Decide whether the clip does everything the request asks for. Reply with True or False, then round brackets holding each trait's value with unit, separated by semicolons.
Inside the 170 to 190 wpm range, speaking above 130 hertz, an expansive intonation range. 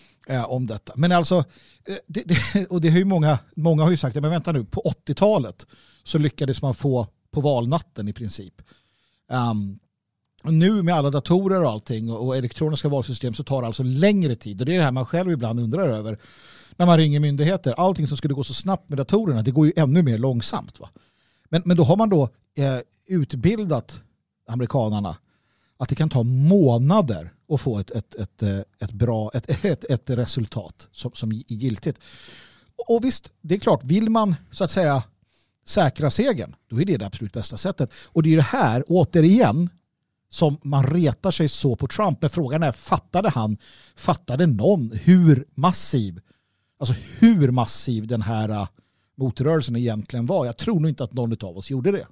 True (180 wpm; 140 Hz; 6.3 semitones)